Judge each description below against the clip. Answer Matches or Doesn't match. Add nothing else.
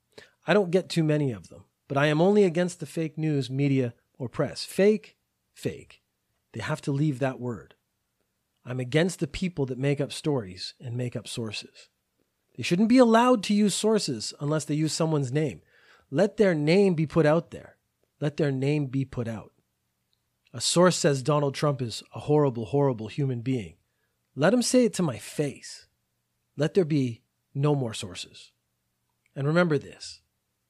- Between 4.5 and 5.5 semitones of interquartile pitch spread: Matches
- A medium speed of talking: Matches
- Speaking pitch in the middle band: Matches